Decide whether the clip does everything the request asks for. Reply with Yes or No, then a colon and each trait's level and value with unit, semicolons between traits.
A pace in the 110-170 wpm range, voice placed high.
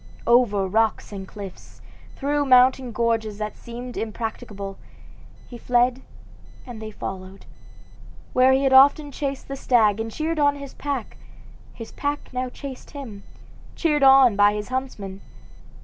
Yes: average, 140 wpm; high, 245 Hz